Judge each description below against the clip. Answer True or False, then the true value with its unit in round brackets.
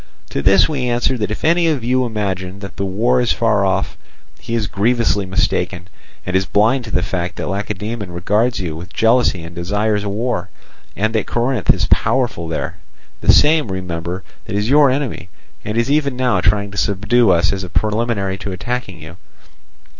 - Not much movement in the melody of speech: False (4.3 semitones)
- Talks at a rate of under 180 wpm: False (185 wpm)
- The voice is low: True (105 Hz)